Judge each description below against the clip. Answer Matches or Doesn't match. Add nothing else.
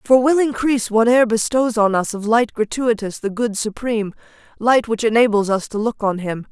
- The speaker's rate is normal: Matches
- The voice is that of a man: Doesn't match